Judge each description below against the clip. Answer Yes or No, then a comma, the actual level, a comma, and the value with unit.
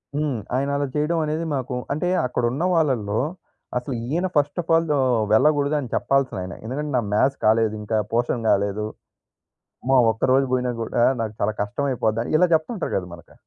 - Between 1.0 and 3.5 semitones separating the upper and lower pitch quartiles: No, average, 4.8 semitones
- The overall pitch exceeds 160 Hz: No, low, 130 Hz